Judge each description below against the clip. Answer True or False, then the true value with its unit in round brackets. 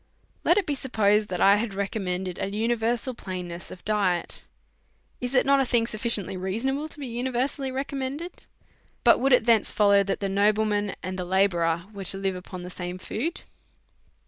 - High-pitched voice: True (210 Hz)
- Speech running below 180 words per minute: False (185 wpm)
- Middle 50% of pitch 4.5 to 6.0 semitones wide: True (4.8 semitones)